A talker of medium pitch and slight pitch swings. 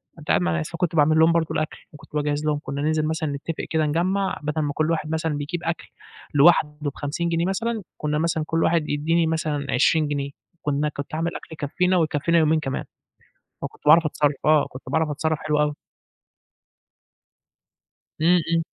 Yes: medium, 155 Hz; narrow, 2.0 semitones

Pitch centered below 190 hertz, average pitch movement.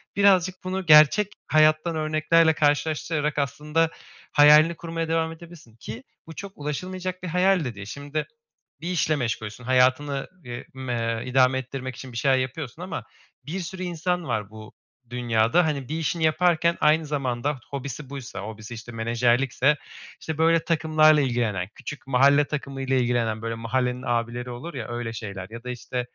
Yes: medium, 140 Hz; average, 4.8 semitones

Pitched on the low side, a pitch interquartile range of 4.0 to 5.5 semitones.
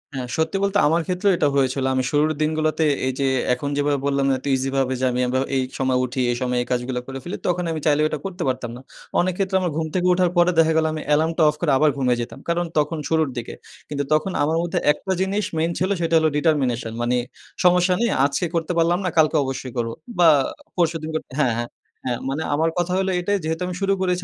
No: medium, 155 Hz; average, 4.7 semitones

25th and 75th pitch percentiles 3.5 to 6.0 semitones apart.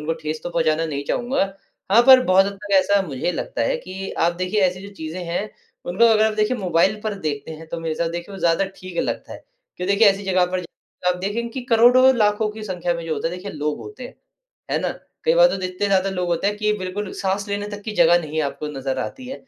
Yes: average, 3.9 semitones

